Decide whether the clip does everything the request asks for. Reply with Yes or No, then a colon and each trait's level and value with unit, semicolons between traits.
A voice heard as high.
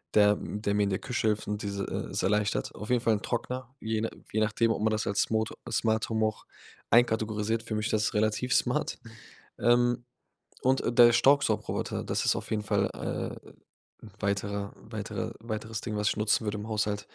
No: low, 110 Hz